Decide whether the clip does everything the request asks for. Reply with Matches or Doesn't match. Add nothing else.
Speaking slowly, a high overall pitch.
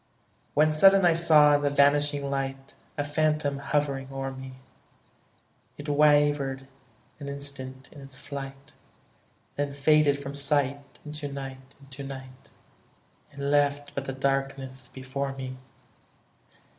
Doesn't match